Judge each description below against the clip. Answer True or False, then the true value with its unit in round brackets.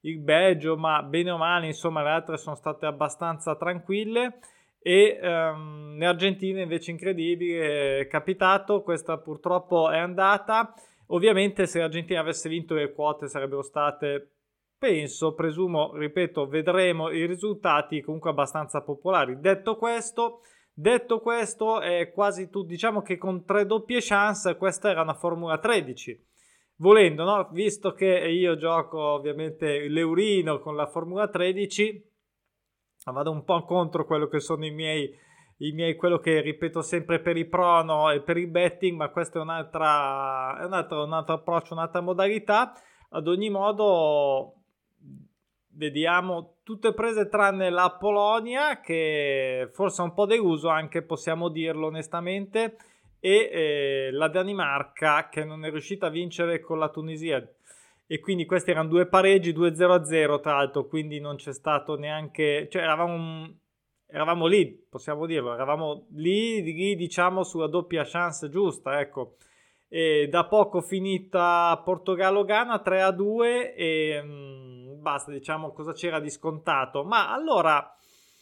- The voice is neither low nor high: True (170 Hz)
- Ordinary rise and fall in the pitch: True (3.7 semitones)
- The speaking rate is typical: True (140 wpm)